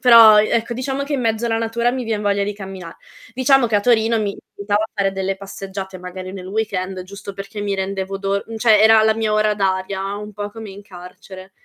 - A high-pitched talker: Yes, high, 205 Hz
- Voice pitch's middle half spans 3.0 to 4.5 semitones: No, narrow, 2.5 semitones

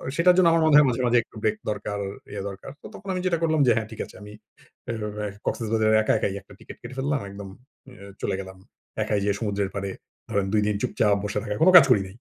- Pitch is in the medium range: No, low, 110 Hz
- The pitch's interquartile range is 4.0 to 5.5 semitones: Yes, average, 5.0 semitones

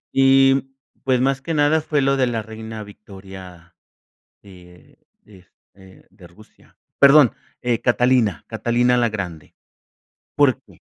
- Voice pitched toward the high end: No, low, 115 Hz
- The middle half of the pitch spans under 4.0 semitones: No, wide, 5.5 semitones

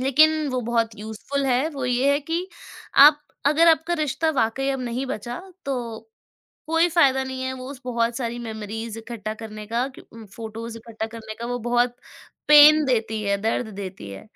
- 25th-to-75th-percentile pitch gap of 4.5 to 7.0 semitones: No, average, 3.9 semitones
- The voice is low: No, high, 245 Hz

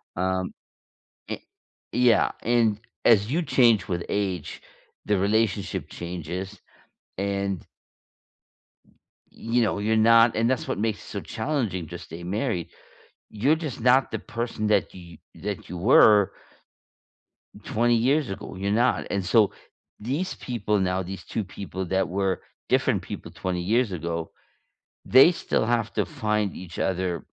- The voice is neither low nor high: No, low, 105 Hz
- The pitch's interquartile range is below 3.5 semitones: No, average, 3.9 semitones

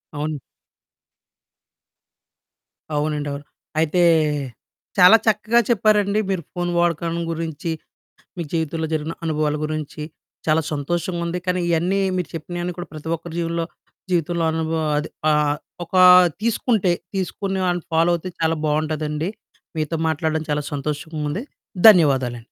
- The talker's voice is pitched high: No, medium, 165 Hz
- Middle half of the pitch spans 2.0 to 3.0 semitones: Yes, narrow, 2.5 semitones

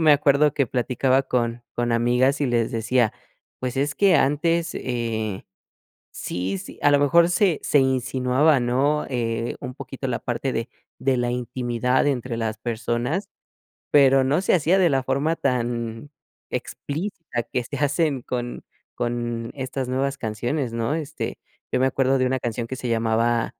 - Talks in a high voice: No, low, 130 Hz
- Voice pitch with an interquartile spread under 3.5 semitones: Yes, average, 3.1 semitones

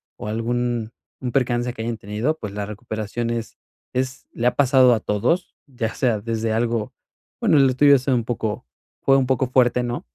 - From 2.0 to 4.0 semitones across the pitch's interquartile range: Yes, narrow, 2.4 semitones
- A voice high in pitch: No, low, 120 Hz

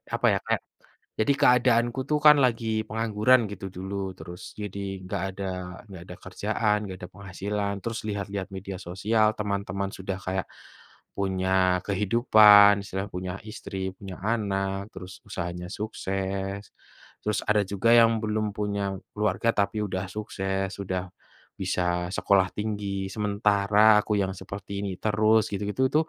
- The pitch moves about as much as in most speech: No, narrow, 1.8 semitones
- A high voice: No, low, 100 Hz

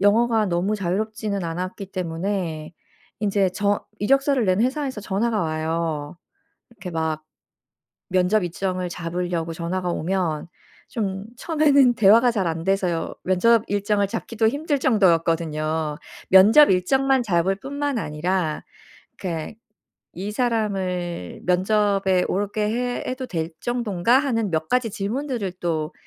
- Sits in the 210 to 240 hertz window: No, high, 195 Hz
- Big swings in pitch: No, average, 4.7 semitones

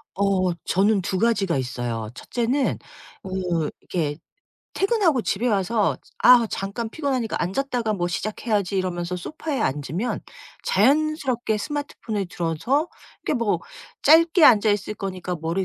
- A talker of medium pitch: No, high, 205 Hz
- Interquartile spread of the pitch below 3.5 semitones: No, wide, 5.6 semitones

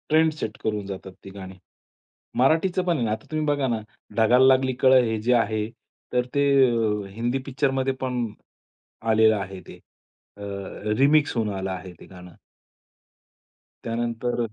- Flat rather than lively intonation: No, average, 4.0 semitones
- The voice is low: Yes, low, 115 Hz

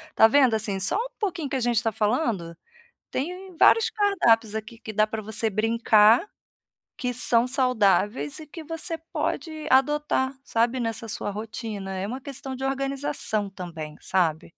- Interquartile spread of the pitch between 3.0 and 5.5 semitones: Yes, average, 4.7 semitones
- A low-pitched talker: No, high, 235 Hz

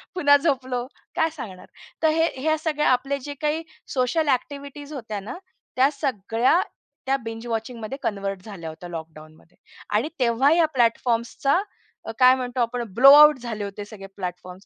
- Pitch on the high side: Yes, high, 245 Hz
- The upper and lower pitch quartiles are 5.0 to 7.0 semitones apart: Yes, average, 5.3 semitones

